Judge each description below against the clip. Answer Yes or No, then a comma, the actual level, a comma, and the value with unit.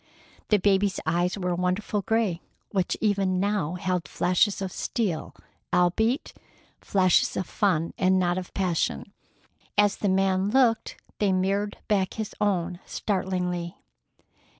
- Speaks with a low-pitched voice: No, high, 190 Hz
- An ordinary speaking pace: No, slow, 125 wpm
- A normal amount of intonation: No, narrow, 2.3 semitones